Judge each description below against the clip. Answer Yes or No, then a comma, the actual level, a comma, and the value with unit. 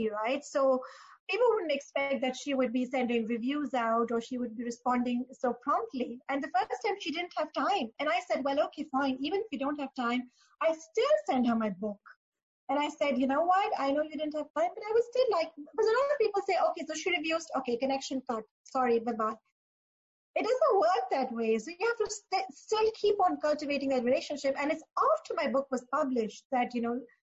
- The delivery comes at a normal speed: No, fast, 225 wpm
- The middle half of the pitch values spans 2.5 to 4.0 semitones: No, average, 4.7 semitones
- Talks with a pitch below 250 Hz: No, very high, 280 Hz